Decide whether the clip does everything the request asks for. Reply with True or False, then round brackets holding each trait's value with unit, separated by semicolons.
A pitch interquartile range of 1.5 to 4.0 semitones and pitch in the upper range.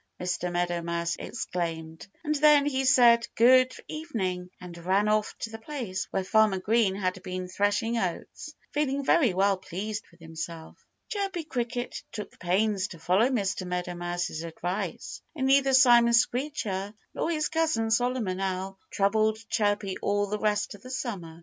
False (5.1 semitones; 205 Hz)